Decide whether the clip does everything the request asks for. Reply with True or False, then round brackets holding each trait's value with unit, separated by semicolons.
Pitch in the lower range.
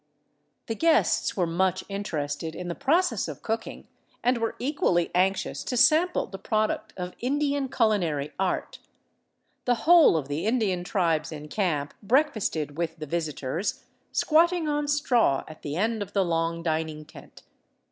False (190 Hz)